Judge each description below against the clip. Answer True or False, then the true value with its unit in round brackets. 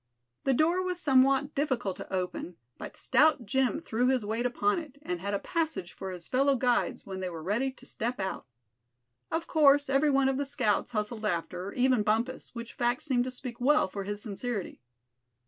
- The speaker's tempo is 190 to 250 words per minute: True (195 wpm)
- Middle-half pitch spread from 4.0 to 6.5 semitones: True (5.1 semitones)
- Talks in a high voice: True (245 Hz)